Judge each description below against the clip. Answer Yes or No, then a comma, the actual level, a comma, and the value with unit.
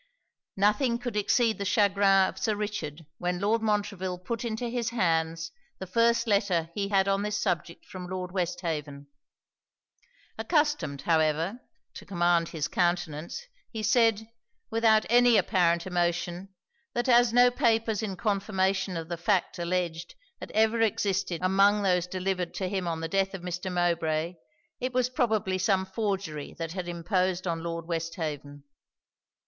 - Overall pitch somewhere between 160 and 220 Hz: Yes, high, 190 Hz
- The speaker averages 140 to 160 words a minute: Yes, average, 150 wpm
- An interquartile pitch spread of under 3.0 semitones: No, average, 3.8 semitones